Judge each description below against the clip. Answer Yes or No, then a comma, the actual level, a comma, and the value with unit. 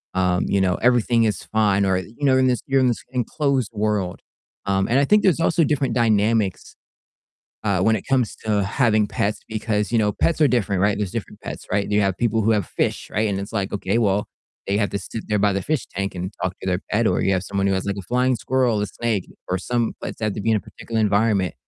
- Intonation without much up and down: No, average, 3.2 semitones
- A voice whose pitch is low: Yes, low, 105 Hz